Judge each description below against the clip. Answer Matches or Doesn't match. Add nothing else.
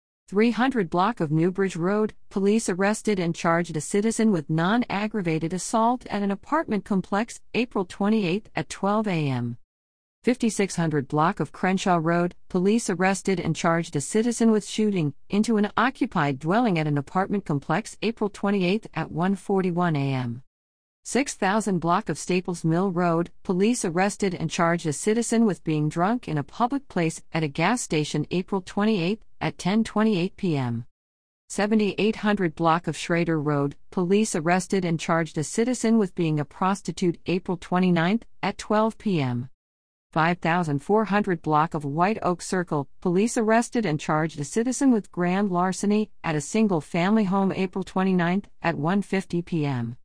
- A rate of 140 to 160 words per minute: Matches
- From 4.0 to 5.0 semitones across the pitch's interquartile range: Matches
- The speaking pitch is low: Doesn't match